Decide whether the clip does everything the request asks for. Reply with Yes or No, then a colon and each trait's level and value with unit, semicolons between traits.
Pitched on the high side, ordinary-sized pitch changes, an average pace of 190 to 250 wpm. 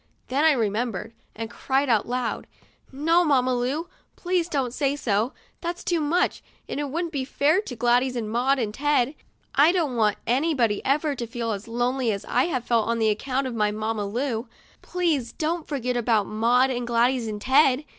Yes: very high, 255 Hz; average, 3.9 semitones; average, 195 wpm